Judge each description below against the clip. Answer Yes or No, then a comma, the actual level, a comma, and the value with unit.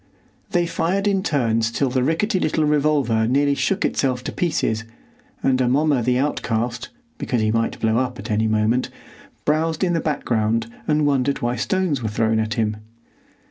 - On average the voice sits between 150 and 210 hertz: No, low, 130 Hz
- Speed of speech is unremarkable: Yes, average, 160 wpm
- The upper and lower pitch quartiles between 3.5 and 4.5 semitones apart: No, wide, 5.4 semitones